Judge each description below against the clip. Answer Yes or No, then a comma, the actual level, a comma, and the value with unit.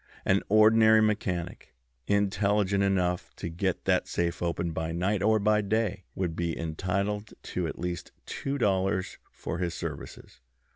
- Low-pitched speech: Yes, very low, 95 Hz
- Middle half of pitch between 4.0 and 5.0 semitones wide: No, average, 3.2 semitones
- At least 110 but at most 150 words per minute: Yes, average, 145 wpm